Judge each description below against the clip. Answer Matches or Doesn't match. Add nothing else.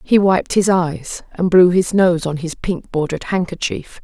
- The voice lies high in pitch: Doesn't match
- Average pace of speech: Matches